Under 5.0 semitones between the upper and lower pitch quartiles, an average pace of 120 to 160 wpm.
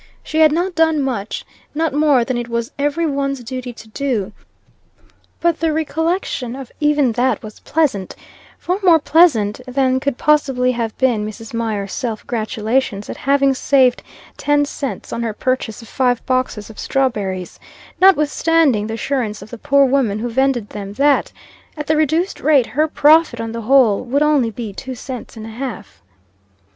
No: average, 4.4 semitones; average, 170 wpm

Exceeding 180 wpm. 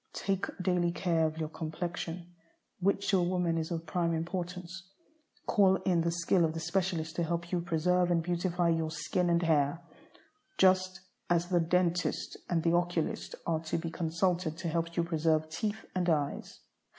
No: average, 175 wpm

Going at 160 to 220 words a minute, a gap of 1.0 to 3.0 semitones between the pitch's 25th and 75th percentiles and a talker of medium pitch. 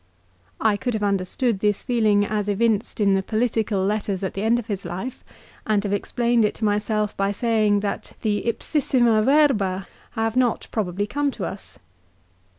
No: average, 170 wpm; narrow, 2.6 semitones; high, 215 Hz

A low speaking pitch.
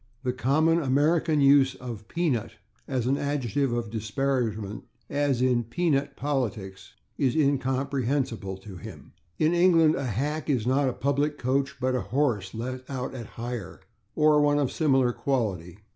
Yes: low, 130 Hz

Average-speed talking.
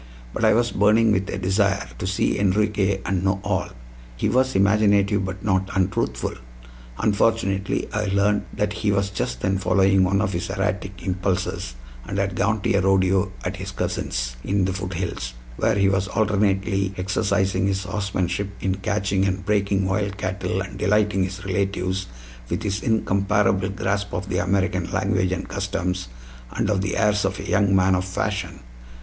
Yes: average, 170 wpm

